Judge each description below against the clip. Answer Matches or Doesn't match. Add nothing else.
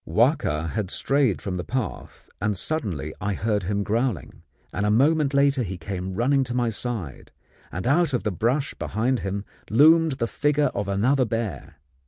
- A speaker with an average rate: Matches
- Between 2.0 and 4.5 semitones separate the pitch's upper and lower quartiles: Doesn't match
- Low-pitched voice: Matches